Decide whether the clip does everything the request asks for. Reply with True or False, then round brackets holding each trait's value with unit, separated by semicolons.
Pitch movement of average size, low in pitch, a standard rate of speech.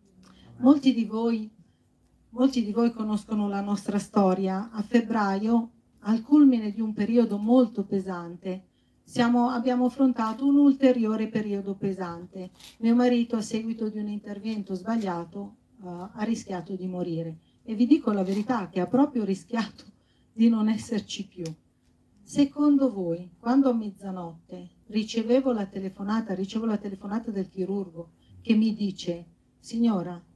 False (3.4 semitones; 215 Hz; 135 wpm)